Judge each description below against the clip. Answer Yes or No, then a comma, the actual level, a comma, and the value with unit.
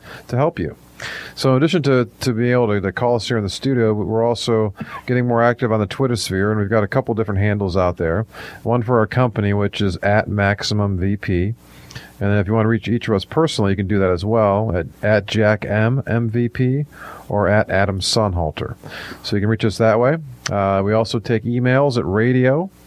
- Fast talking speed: Yes, fast, 225 wpm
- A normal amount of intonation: Yes, average, 3.2 semitones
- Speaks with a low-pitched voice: Yes, low, 110 Hz